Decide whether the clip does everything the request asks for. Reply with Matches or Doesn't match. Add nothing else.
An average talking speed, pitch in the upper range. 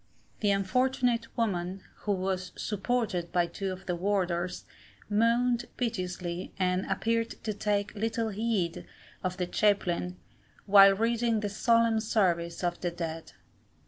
Doesn't match